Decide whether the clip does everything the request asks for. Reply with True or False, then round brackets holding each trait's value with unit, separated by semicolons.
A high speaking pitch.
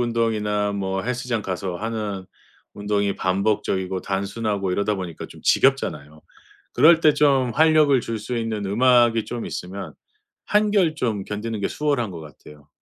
False (105 Hz)